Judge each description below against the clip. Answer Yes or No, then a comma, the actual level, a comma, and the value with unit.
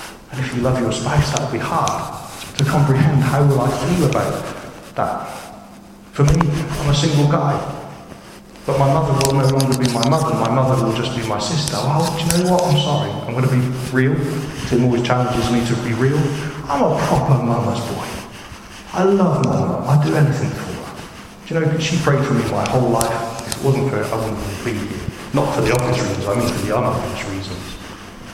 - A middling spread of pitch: Yes, average, 3.8 semitones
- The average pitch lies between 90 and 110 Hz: No, low, 135 Hz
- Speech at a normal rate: No, fast, 215 wpm